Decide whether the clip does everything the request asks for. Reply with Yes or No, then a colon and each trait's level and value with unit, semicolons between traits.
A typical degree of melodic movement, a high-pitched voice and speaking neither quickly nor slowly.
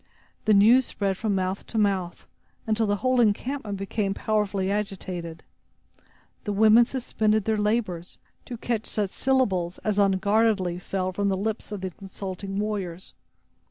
No: narrow, 2.3 semitones; high, 205 Hz; average, 145 wpm